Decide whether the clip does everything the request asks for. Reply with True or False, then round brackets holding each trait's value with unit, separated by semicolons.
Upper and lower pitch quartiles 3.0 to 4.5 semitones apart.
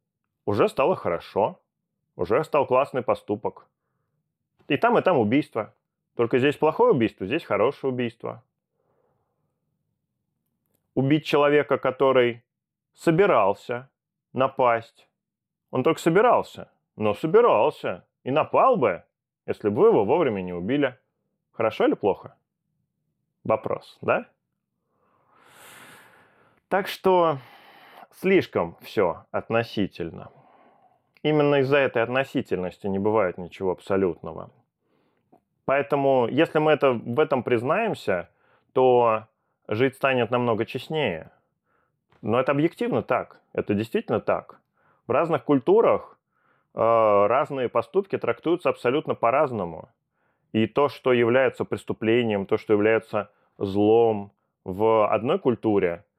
False (4.9 semitones)